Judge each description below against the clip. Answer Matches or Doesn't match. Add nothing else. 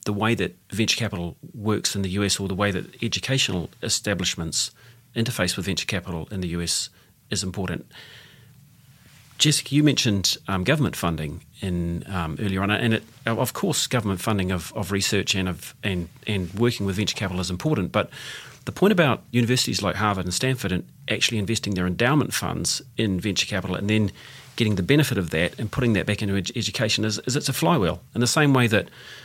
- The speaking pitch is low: Matches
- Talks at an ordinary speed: Matches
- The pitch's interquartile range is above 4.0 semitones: Matches